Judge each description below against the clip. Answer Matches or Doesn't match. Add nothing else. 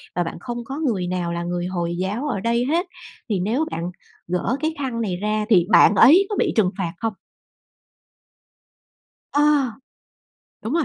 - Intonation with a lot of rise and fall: Matches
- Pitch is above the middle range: Matches